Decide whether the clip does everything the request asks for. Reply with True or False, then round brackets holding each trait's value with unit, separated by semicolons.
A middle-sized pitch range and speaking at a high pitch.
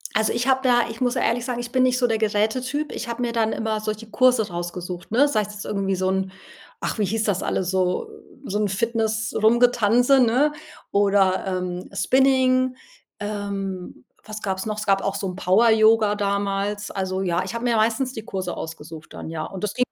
True (3.7 semitones; 215 Hz)